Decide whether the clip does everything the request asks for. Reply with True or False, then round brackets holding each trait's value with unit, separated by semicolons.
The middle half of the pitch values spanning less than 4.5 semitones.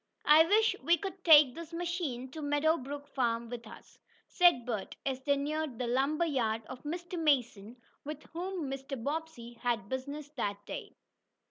False (4.8 semitones)